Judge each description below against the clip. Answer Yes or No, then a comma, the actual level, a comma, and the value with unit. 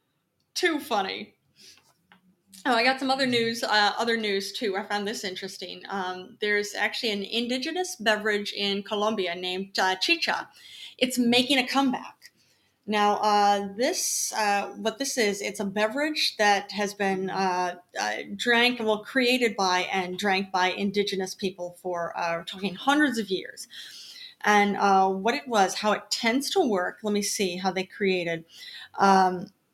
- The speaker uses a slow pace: No, average, 160 wpm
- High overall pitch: Yes, high, 205 Hz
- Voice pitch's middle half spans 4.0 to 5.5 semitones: No, average, 3.5 semitones